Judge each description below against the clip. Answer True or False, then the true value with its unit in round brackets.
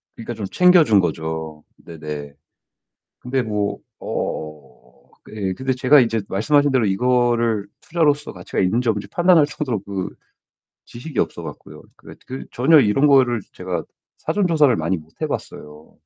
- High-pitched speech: False (115 Hz)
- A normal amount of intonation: False (6.6 semitones)